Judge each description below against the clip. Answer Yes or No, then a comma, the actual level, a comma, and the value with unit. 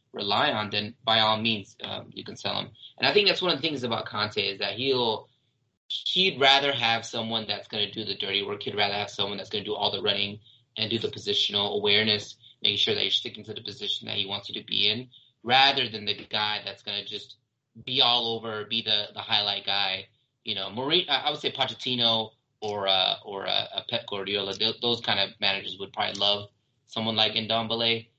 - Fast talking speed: Yes, fast, 225 wpm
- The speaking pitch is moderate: No, low, 110 Hz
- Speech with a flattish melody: No, average, 3.0 semitones